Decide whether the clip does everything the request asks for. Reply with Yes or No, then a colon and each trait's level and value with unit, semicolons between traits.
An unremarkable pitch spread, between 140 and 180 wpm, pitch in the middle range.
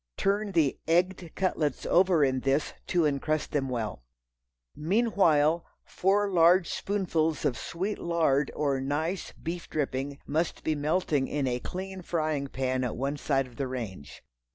Yes: average, 4.6 semitones; average, 150 wpm; medium, 155 Hz